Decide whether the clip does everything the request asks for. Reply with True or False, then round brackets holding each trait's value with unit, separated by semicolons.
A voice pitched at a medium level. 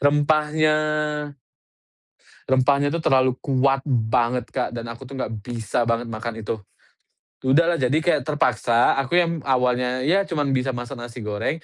False (130 Hz)